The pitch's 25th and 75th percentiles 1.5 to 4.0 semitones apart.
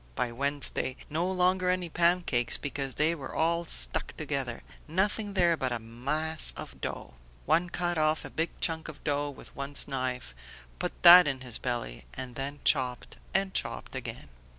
No: average, 4.8 semitones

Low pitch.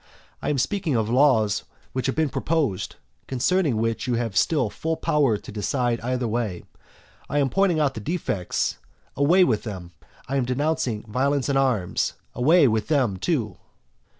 Yes: low, 130 Hz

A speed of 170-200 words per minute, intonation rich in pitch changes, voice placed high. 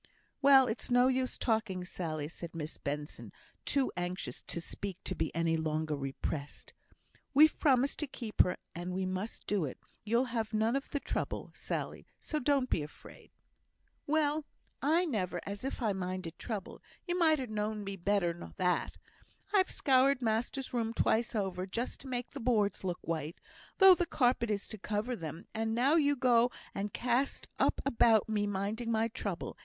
Yes: average, 175 wpm; wide, 5.8 semitones; high, 220 Hz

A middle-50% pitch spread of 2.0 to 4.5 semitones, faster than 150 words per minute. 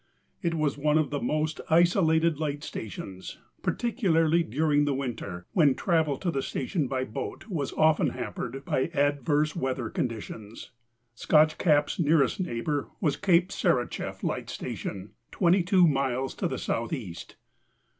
No: average, 4.0 semitones; slow, 135 wpm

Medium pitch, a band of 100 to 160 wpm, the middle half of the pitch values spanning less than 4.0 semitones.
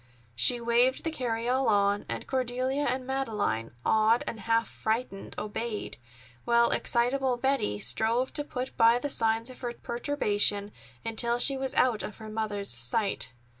No: high, 235 Hz; average, 150 wpm; average, 3.2 semitones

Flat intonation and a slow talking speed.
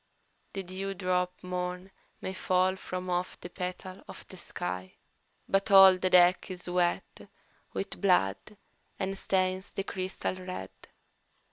Yes: narrow, 0.9 semitones; slow, 130 wpm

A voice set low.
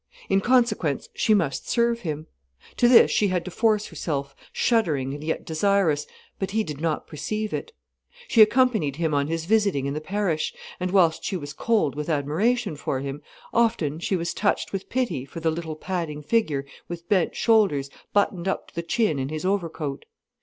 No: medium, 170 Hz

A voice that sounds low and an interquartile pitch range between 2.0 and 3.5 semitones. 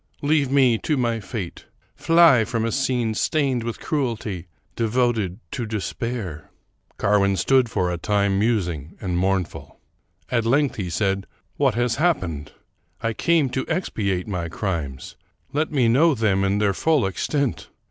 No: low, 115 Hz; average, 5.3 semitones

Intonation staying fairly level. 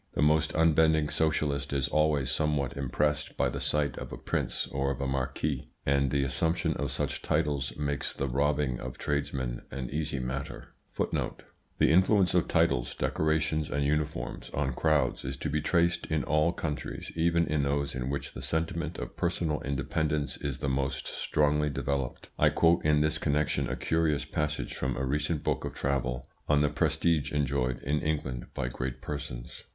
Yes: narrow, 2.3 semitones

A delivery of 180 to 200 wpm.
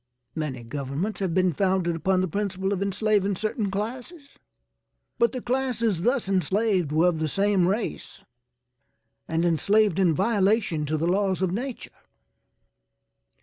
No: average, 140 wpm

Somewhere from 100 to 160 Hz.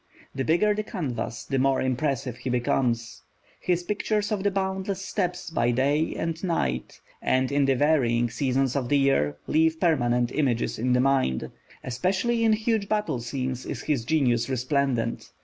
Yes: low, 135 Hz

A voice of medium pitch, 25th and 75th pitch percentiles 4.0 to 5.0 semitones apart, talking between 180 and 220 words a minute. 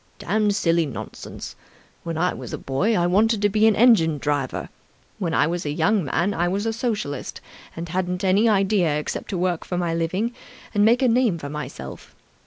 Yes: medium, 180 Hz; average, 4.6 semitones; average, 195 wpm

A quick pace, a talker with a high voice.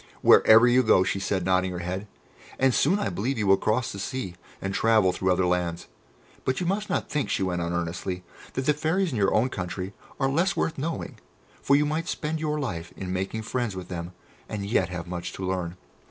No: fast, 220 wpm; low, 100 Hz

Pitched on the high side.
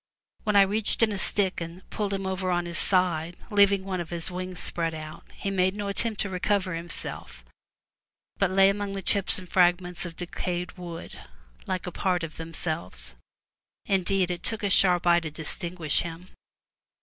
No: medium, 180 Hz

